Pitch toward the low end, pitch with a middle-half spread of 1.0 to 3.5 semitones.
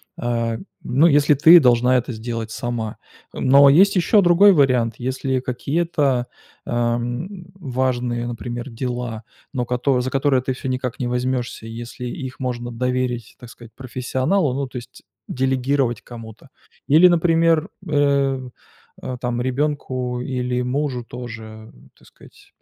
Yes: low, 125 Hz; narrow, 2.5 semitones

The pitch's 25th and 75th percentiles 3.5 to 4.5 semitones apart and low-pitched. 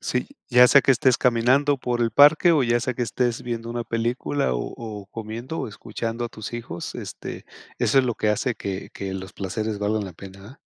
No: average, 2.9 semitones; low, 115 Hz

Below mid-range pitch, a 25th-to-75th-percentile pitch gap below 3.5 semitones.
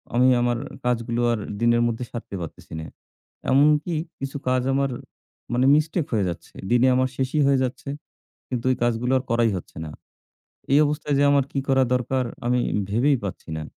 Yes: low, 125 Hz; average, 2.8 semitones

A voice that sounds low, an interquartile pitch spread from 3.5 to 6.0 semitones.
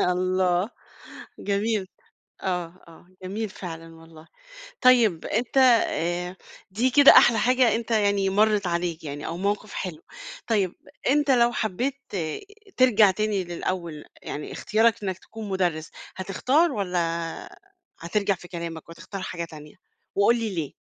No: high, 190 Hz; average, 4.4 semitones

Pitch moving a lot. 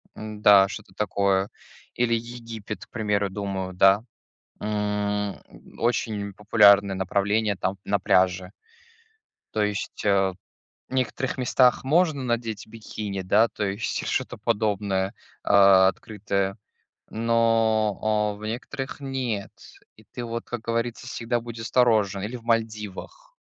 No: average, 2.7 semitones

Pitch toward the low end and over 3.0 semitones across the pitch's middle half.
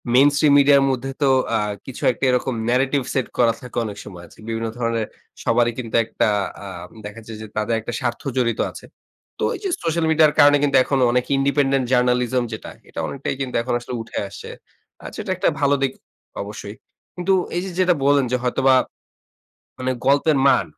Yes: low, 130 Hz; average, 3.4 semitones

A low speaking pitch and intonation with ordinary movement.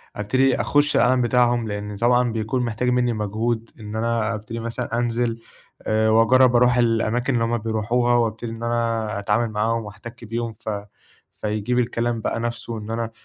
No: low, 115 Hz; narrow, 1.6 semitones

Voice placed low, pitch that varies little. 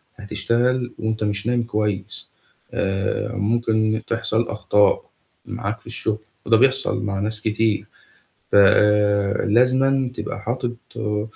Yes: low, 110 Hz; narrow, 2.3 semitones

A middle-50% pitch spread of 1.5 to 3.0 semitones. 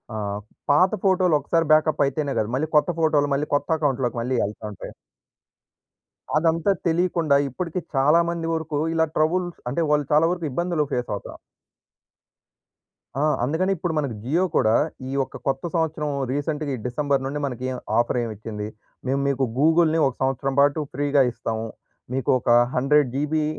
No: average, 3.4 semitones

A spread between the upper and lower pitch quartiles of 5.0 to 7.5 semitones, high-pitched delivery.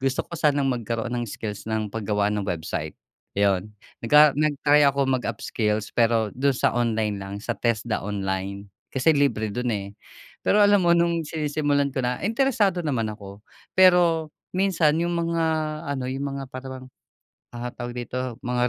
No: wide, 5.6 semitones; low, 125 Hz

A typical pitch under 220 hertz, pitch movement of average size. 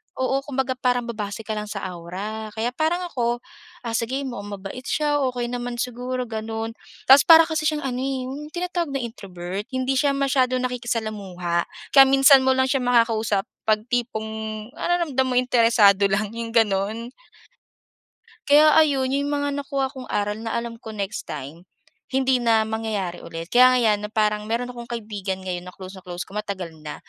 No: high, 235 Hz; average, 3.9 semitones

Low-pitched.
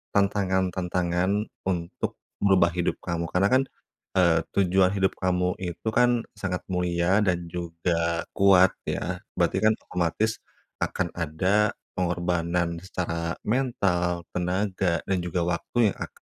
Yes: very low, 90 Hz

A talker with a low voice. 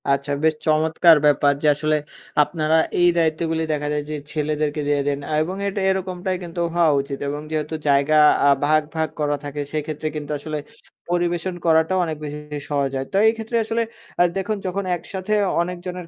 No: medium, 160 Hz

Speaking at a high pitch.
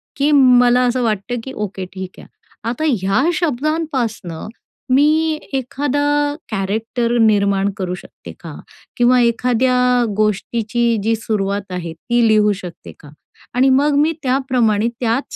Yes: high, 240 Hz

